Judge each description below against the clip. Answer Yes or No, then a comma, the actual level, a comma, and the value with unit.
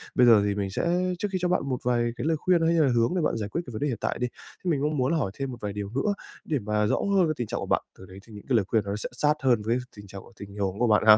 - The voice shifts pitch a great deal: Yes, wide, 6.4 semitones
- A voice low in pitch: Yes, low, 120 Hz